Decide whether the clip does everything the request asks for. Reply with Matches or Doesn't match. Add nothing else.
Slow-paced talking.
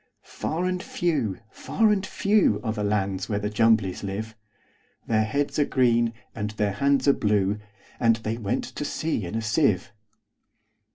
Doesn't match